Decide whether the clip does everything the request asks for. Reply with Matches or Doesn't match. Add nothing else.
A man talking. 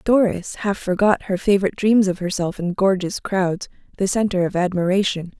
Doesn't match